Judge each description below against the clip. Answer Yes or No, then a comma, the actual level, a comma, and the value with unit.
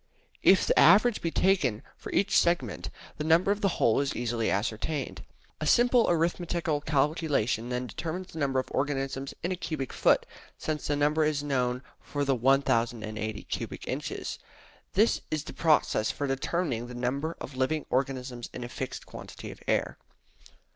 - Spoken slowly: No, average, 165 wpm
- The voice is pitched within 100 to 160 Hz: Yes, medium, 140 Hz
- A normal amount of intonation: Yes, average, 4.7 semitones